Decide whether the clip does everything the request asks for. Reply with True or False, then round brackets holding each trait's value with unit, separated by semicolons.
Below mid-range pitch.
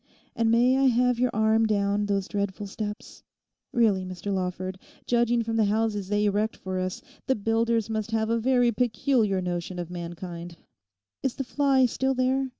False (220 Hz)